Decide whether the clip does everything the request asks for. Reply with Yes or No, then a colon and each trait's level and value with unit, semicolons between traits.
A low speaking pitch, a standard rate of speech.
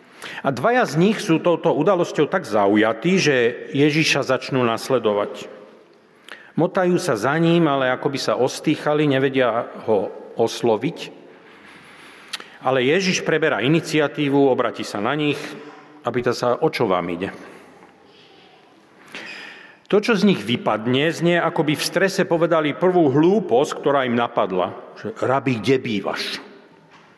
No: medium, 150 Hz; average, 130 wpm